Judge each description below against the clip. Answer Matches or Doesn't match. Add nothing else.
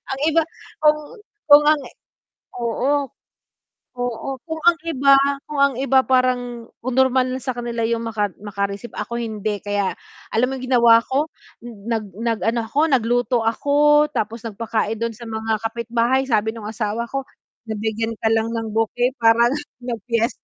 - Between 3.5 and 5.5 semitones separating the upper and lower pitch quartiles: Doesn't match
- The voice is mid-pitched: Doesn't match